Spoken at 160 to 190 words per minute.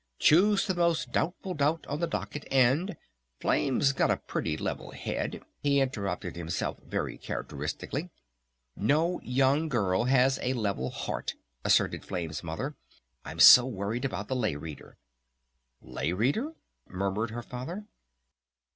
No: slow, 135 wpm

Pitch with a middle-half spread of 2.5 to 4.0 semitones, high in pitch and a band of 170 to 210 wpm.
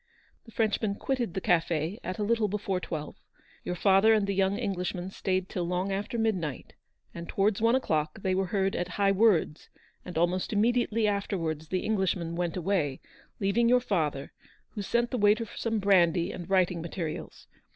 Yes: average, 3.3 semitones; high, 195 Hz; average, 175 wpm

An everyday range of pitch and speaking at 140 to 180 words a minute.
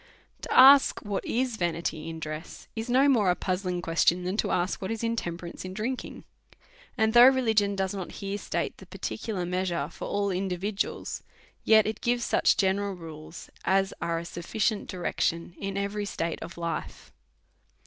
Yes: average, 4.0 semitones; average, 170 wpm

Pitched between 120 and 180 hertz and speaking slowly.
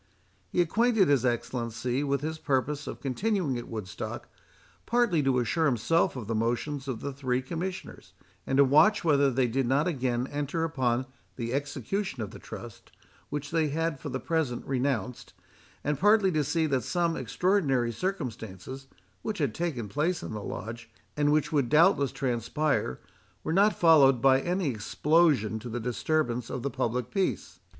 No: medium, 140 Hz; average, 165 wpm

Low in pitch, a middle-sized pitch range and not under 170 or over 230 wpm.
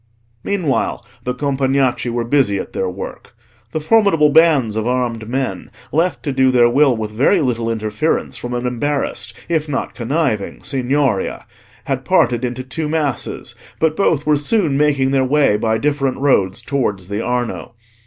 No: low, 130 Hz; average, 3.9 semitones; average, 160 wpm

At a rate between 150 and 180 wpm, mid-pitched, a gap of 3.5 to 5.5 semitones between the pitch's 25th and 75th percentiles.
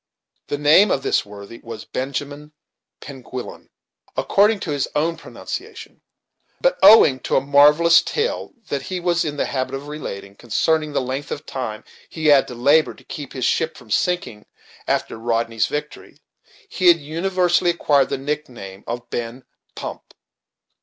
Yes: average, 160 wpm; medium, 145 Hz; average, 4.5 semitones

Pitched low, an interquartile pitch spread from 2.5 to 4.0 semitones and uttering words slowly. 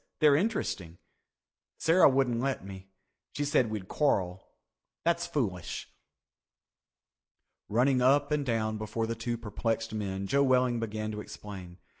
No: low, 115 Hz; average, 4.8 semitones; slow, 130 wpm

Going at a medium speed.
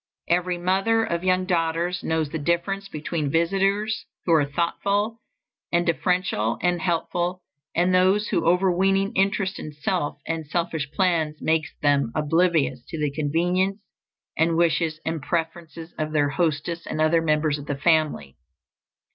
Yes: average, 145 wpm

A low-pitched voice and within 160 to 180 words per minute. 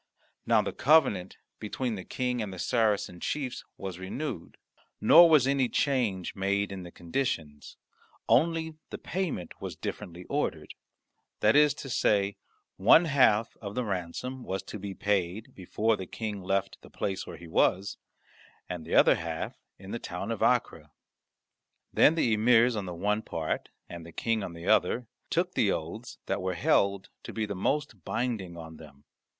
Yes: low, 100 Hz; average, 170 wpm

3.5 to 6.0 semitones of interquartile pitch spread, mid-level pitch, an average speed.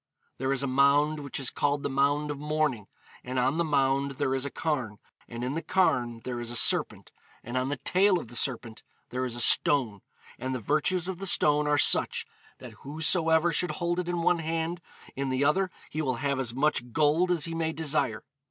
No: average, 3.9 semitones; medium, 145 Hz; fast, 215 wpm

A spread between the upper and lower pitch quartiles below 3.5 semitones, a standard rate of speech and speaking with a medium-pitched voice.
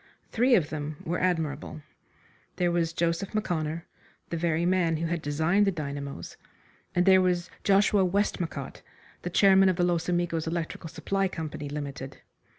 Yes: average, 2.8 semitones; average, 155 wpm; medium, 170 Hz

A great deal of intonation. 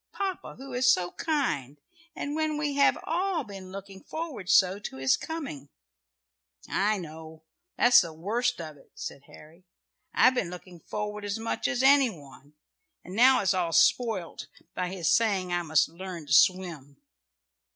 Yes: wide, 7.1 semitones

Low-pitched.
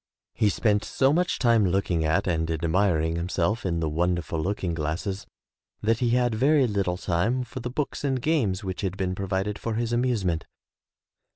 Yes: low, 100 Hz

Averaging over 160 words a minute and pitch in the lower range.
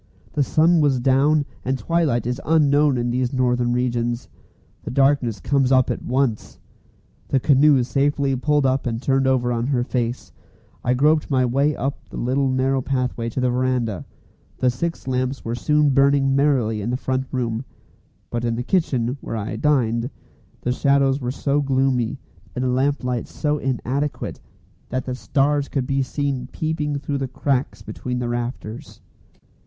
Yes: average, 170 wpm; low, 130 Hz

